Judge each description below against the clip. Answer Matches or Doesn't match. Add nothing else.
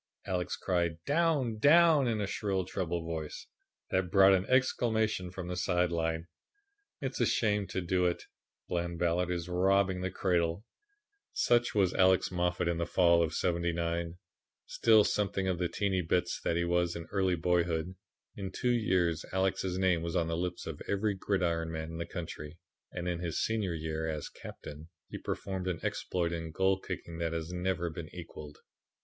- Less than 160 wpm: Doesn't match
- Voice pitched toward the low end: Matches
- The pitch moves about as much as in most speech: Doesn't match